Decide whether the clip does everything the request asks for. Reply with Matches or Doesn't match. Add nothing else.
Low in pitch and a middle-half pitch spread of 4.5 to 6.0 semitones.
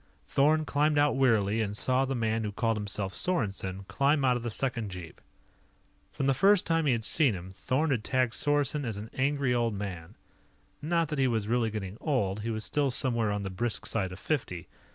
Matches